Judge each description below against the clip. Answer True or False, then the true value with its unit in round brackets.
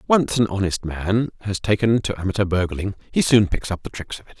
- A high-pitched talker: False (100 Hz)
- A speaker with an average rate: False (230 wpm)